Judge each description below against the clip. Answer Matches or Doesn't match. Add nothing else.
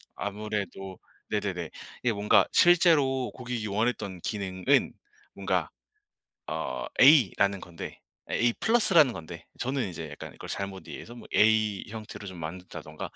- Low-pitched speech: Matches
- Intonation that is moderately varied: Matches